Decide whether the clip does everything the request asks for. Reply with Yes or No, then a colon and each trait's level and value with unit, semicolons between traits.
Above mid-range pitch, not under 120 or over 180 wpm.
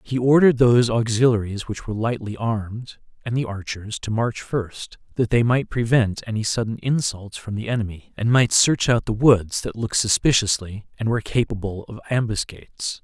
No: low, 115 Hz; average, 175 wpm